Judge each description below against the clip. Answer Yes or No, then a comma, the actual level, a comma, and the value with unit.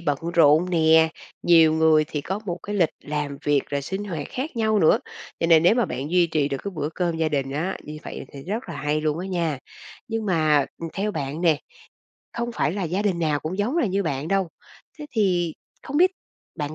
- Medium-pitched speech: Yes, medium, 165 Hz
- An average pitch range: Yes, average, 4.3 semitones